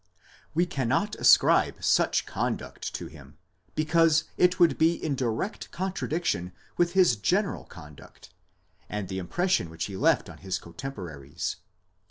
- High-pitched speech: No, low, 135 Hz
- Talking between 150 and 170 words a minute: No, slow, 135 wpm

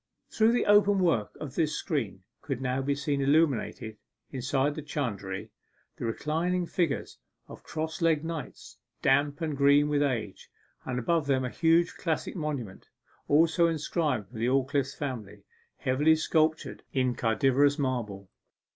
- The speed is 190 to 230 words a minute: No, average, 145 wpm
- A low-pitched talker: No, medium, 145 Hz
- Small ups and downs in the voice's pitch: No, average, 3.8 semitones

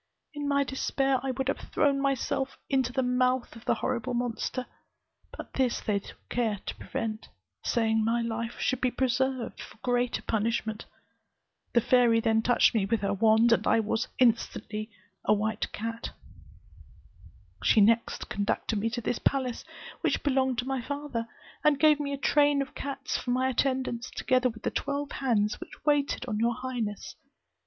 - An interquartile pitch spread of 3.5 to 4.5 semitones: No, average, 2.8 semitones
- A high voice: Yes, high, 245 Hz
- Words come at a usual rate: Yes, average, 170 wpm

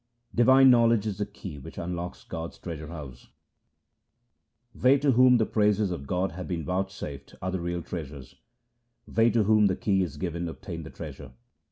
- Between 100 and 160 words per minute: No, average, 180 wpm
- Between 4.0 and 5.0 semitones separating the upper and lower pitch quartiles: Yes, average, 4.6 semitones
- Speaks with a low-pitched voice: Yes, very low, 95 Hz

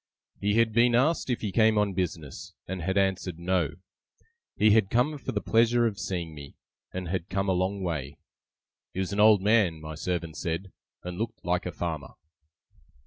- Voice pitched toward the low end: Yes, very low, 95 Hz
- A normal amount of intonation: Yes, average, 4.0 semitones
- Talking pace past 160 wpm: Yes, average, 190 wpm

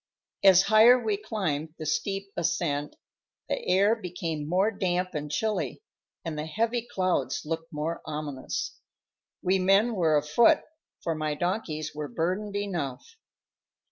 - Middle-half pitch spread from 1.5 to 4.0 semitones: No, average, 4.7 semitones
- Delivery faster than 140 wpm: No, slow, 135 wpm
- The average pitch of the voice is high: No, medium, 180 Hz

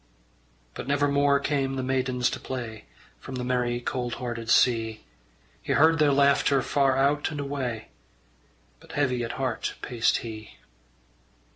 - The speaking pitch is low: Yes, low, 130 Hz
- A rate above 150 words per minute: No, average, 145 wpm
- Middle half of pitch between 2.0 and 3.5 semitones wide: Yes, average, 2.7 semitones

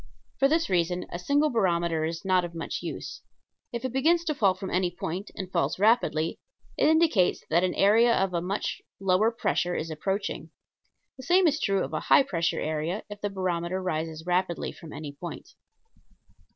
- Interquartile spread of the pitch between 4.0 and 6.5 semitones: Yes, average, 5.1 semitones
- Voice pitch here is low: No, medium, 185 Hz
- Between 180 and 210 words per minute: Yes, average, 185 wpm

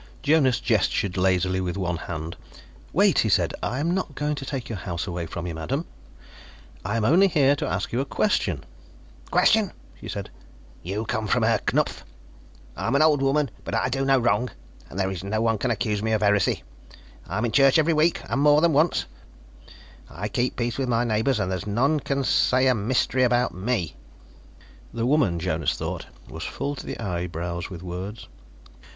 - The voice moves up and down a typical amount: No, wide, 6.6 semitones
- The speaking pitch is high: No, low, 115 Hz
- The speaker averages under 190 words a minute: No, average, 195 wpm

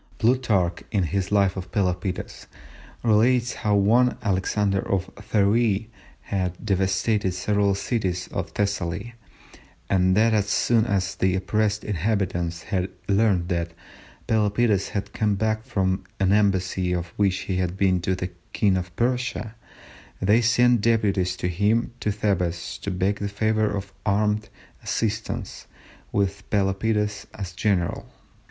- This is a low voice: Yes, low, 100 Hz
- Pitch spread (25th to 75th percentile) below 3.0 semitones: Yes, narrow, 2.6 semitones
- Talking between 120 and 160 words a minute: Yes, slow, 135 wpm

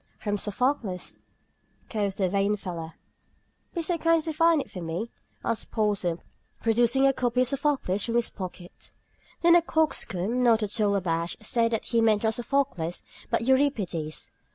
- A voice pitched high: Yes, high, 225 Hz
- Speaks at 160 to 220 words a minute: Yes, average, 165 wpm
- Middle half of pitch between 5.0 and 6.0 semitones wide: Yes, wide, 5.6 semitones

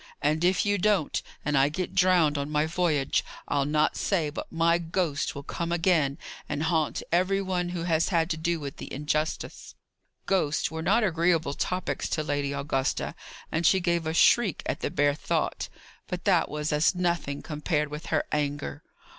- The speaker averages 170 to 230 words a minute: Yes, average, 180 wpm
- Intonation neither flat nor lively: Yes, average, 3.0 semitones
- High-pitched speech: No, medium, 160 Hz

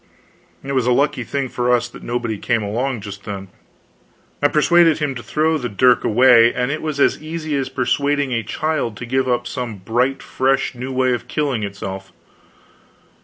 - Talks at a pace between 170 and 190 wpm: Yes, average, 185 wpm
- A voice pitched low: Yes, low, 125 Hz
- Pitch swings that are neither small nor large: Yes, average, 3.3 semitones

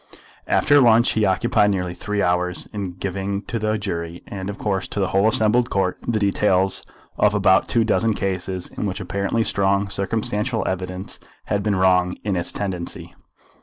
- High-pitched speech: No, low, 100 Hz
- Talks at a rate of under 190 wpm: Yes, average, 170 wpm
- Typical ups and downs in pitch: No, narrow, 2.3 semitones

